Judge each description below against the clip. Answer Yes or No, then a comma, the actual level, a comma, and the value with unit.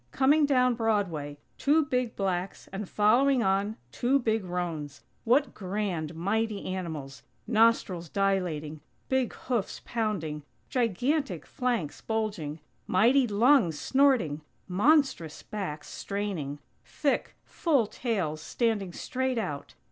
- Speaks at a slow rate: Yes, slow, 110 wpm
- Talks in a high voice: Yes, high, 210 Hz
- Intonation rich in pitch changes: Yes, wide, 6.3 semitones